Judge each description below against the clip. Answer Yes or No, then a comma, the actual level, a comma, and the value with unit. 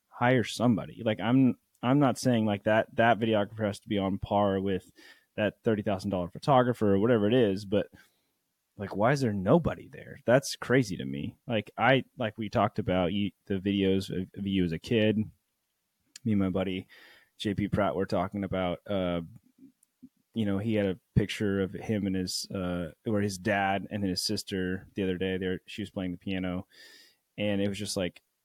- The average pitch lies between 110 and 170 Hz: No, low, 100 Hz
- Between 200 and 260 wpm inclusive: No, average, 190 wpm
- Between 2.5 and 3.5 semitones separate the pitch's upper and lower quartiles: Yes, average, 2.9 semitones